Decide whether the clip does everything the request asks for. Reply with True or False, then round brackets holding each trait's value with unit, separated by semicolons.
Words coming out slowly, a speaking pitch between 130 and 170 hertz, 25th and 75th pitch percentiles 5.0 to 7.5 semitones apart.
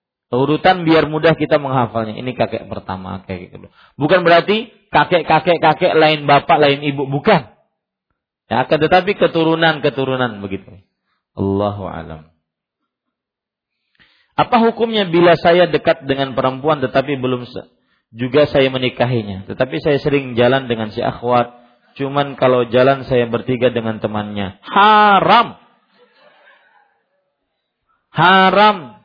False (110 wpm; 135 Hz; 5.4 semitones)